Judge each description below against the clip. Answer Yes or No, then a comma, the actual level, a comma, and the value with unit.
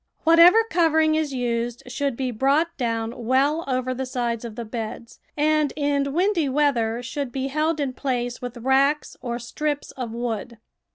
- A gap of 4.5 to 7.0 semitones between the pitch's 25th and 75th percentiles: No, average, 3.8 semitones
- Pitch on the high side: Yes, very high, 265 Hz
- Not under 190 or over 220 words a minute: No, average, 165 wpm